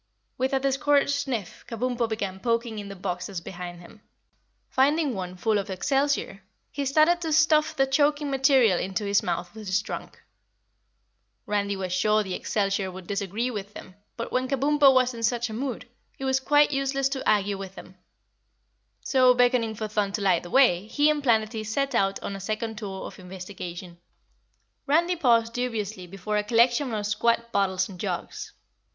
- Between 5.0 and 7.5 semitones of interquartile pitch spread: Yes, wide, 5.4 semitones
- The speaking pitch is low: No, high, 225 Hz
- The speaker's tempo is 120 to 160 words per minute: No, average, 175 wpm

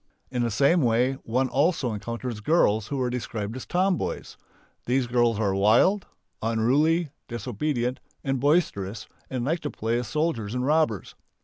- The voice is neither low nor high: No, low, 125 Hz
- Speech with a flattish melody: No, average, 4.6 semitones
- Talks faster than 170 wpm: No, average, 145 wpm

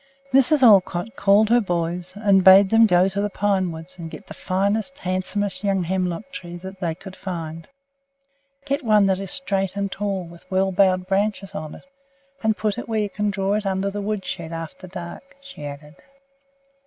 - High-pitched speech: Yes, high, 195 Hz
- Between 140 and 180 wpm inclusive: No, average, 190 wpm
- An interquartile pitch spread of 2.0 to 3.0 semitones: Yes, narrow, 2.5 semitones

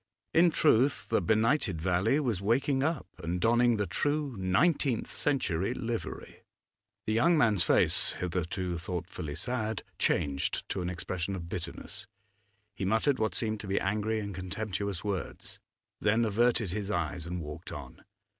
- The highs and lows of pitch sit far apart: No, average, 4.8 semitones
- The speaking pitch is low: Yes, low, 105 Hz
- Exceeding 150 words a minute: No, average, 145 wpm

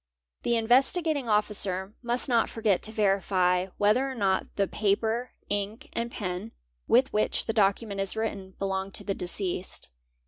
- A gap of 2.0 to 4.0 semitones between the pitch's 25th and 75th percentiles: Yes, average, 3.1 semitones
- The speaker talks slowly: No, average, 165 wpm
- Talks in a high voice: Yes, high, 210 Hz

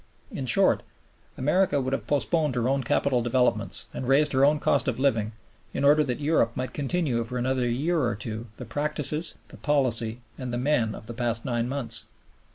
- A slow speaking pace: No, average, 190 wpm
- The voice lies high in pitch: No, low, 130 Hz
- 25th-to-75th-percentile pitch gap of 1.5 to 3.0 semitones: No, average, 3.4 semitones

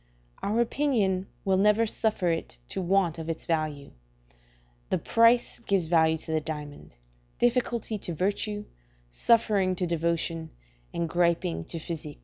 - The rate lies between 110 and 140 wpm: Yes, slow, 135 wpm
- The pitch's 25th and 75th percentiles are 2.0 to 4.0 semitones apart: No, average, 4.6 semitones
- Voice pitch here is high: No, medium, 180 Hz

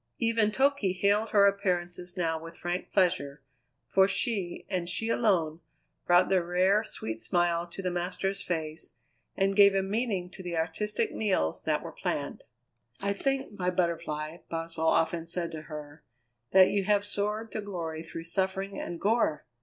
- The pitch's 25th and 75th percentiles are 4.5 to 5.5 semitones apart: No, average, 3.2 semitones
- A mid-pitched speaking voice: Yes, medium, 180 Hz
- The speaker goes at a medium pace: Yes, average, 160 wpm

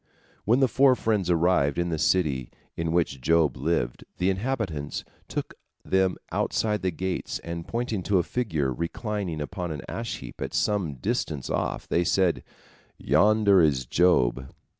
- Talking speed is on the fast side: No, average, 155 wpm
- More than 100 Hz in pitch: No, very low, 90 Hz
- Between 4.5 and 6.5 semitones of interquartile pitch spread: Yes, average, 5.0 semitones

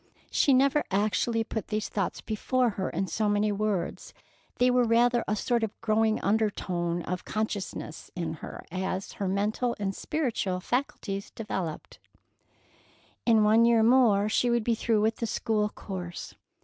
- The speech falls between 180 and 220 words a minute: No, average, 155 wpm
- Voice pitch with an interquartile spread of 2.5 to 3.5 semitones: Yes, average, 3.1 semitones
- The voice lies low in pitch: No, high, 215 Hz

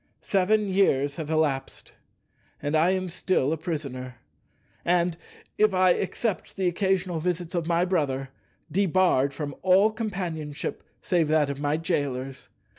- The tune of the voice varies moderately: Yes, average, 4.3 semitones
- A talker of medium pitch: Yes, medium, 165 Hz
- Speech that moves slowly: Yes, slow, 125 wpm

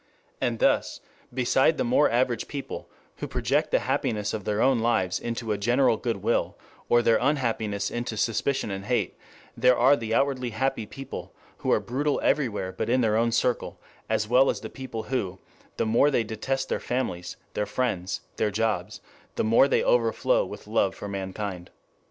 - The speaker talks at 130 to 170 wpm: No, average, 180 wpm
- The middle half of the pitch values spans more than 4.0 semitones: No, average, 3.4 semitones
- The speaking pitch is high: No, low, 115 Hz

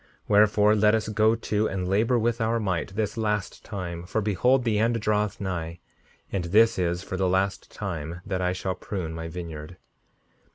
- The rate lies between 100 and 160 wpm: No, average, 190 wpm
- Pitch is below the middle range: Yes, low, 100 Hz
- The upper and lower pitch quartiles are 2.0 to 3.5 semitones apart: Yes, average, 3.2 semitones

